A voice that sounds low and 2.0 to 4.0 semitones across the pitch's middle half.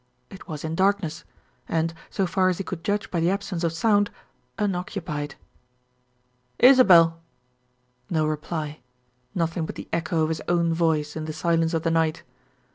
No: medium, 165 Hz; average, 2.8 semitones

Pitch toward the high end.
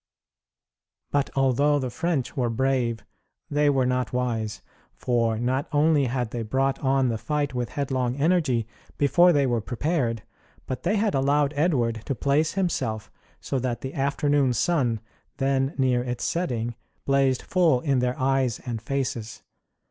No: low, 130 Hz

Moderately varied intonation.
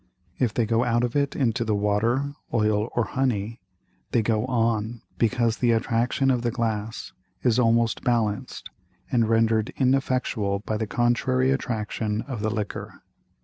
No: narrow, 2.1 semitones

